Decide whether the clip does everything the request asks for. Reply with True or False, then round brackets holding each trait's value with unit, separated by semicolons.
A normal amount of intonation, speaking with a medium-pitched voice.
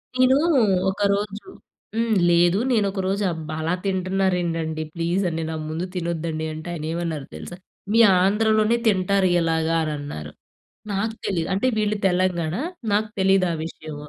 True (3.5 semitones; 180 Hz)